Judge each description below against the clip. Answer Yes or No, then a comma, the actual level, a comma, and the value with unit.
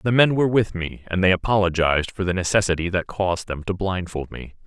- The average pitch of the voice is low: Yes, very low, 95 Hz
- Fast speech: Yes, fast, 220 wpm